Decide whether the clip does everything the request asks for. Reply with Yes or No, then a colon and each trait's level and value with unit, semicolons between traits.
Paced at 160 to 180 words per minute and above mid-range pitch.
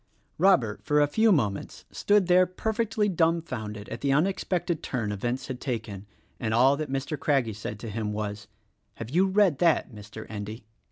No: average, 170 wpm; low, 135 Hz